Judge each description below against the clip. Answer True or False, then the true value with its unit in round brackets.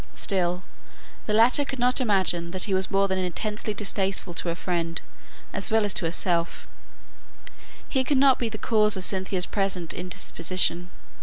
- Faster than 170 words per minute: False (165 wpm)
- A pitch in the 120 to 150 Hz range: False (190 Hz)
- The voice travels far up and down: False (3.3 semitones)